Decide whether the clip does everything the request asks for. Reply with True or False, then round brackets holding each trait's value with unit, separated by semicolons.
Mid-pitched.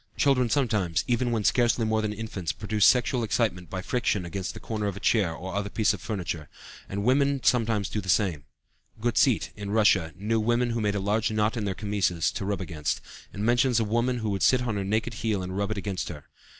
False (105 Hz)